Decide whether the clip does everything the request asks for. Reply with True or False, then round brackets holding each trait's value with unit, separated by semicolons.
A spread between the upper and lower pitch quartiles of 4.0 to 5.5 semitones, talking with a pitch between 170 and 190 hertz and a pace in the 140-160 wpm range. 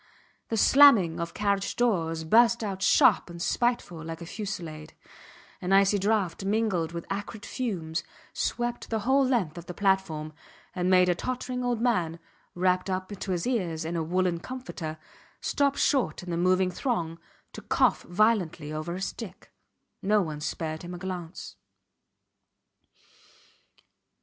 True (4.6 semitones; 185 Hz; 150 wpm)